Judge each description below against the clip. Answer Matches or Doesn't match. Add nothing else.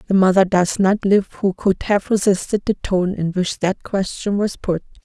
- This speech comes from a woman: Matches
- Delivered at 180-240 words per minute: Matches